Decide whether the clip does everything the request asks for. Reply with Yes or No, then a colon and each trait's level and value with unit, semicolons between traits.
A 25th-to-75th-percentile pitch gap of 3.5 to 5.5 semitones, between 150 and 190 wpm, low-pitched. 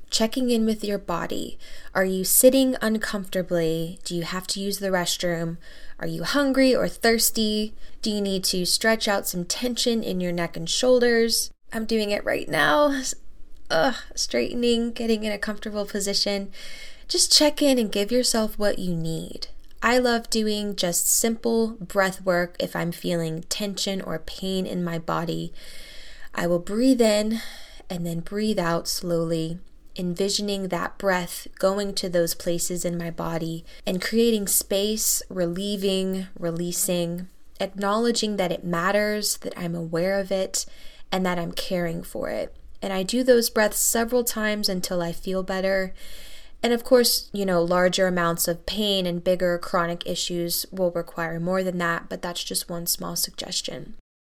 No: average, 4.1 semitones; average, 160 wpm; high, 190 Hz